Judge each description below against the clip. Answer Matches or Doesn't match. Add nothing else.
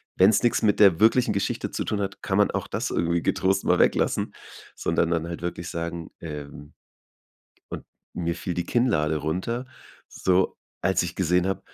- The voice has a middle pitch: Doesn't match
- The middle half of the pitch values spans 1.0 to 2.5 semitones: Doesn't match